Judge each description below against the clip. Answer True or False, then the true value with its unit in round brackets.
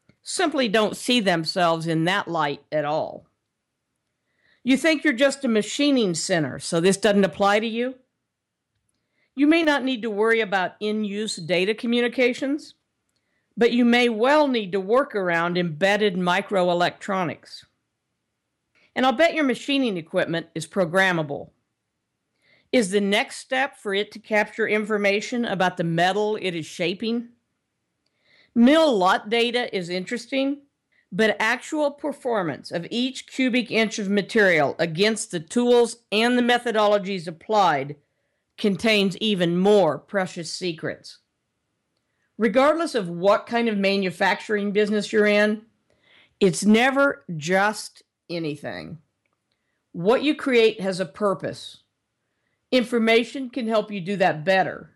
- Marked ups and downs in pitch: False (4.7 semitones)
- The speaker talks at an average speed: False (130 wpm)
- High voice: True (210 Hz)